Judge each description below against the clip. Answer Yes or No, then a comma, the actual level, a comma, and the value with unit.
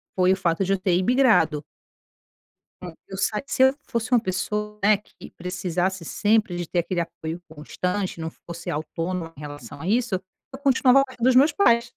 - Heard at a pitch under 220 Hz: Yes, high, 190 Hz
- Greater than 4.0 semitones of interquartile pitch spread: Yes, average, 5.3 semitones